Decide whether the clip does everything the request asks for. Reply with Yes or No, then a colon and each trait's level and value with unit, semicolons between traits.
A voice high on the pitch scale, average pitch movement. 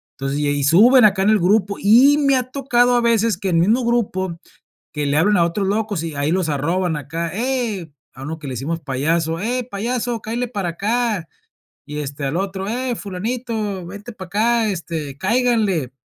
No: high, 195 Hz; wide, 6.1 semitones